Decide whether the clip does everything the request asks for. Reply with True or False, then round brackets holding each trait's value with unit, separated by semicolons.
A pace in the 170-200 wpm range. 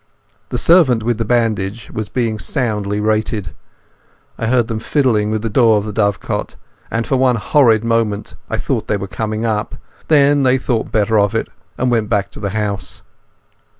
True (185 wpm)